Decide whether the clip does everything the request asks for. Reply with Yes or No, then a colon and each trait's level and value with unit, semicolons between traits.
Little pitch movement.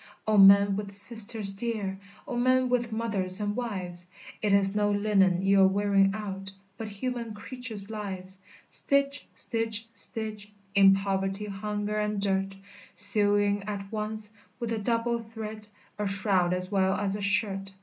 Yes: narrow, 2.0 semitones